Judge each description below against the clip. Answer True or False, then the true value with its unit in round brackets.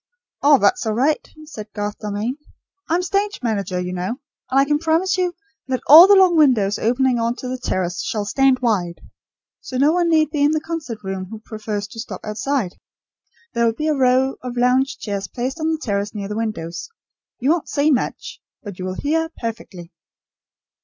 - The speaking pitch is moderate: False (250 Hz)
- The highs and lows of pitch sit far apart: True (6.4 semitones)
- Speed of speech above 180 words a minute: True (195 wpm)